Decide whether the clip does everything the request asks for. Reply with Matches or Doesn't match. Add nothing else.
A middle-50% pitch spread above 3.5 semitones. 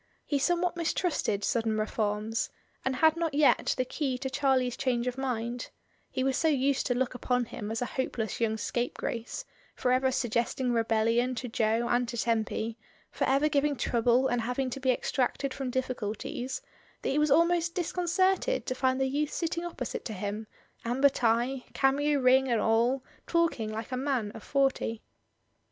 Doesn't match